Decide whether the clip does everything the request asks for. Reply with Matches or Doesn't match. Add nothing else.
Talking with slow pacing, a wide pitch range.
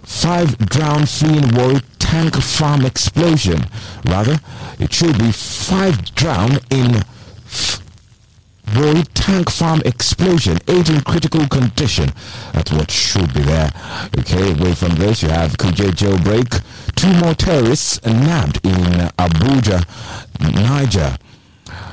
Matches